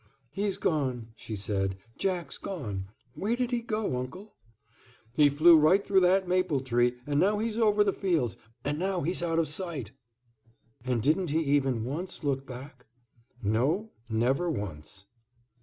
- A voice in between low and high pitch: Yes, medium, 150 Hz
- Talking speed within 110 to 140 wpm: No, average, 155 wpm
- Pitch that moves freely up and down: Yes, wide, 7.1 semitones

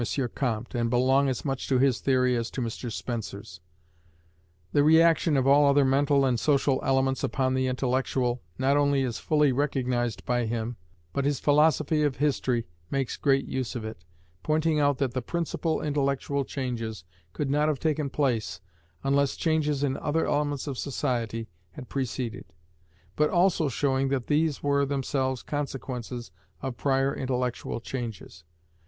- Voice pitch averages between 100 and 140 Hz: Yes, low, 135 Hz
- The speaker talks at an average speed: Yes, average, 155 wpm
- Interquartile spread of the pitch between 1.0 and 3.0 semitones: Yes, narrow, 2.6 semitones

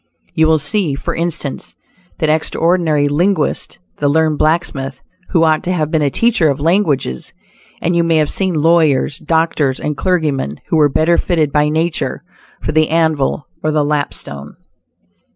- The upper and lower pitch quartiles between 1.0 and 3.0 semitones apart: Yes, narrow, 2.5 semitones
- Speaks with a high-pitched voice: No, medium, 155 Hz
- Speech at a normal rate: Yes, average, 160 wpm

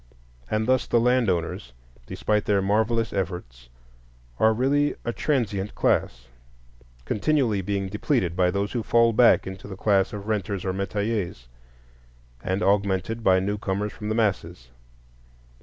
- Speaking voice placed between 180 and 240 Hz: No, low, 100 Hz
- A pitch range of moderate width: Yes, average, 3.0 semitones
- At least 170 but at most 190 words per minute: No, average, 140 wpm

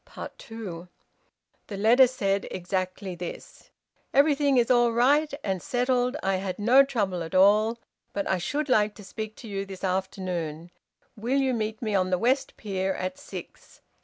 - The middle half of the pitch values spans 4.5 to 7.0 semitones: Yes, average, 4.8 semitones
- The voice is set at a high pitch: Yes, high, 210 Hz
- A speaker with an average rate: Yes, average, 160 wpm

